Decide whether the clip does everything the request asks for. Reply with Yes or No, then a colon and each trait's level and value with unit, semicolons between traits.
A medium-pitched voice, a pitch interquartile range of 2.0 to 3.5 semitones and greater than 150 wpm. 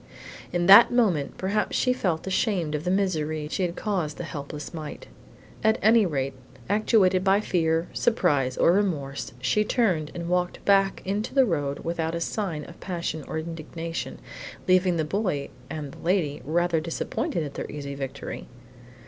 No: medium, 170 Hz; average, 4.3 semitones; average, 165 wpm